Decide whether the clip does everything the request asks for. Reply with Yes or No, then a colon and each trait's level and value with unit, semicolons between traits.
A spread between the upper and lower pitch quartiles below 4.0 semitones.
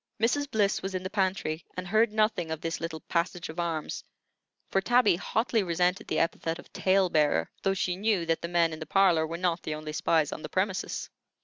Yes: average, 3.0 semitones